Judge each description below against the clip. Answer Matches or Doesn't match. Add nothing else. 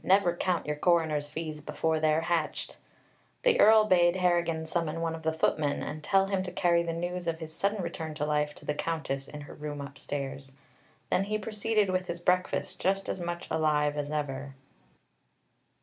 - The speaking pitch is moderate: Matches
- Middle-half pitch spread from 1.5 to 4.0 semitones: Matches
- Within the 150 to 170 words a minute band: Doesn't match